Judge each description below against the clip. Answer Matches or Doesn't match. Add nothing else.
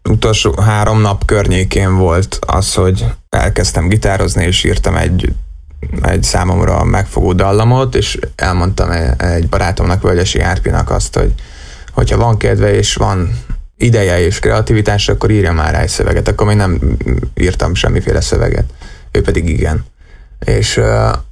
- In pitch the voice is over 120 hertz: Doesn't match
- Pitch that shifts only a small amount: Doesn't match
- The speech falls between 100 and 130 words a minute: Doesn't match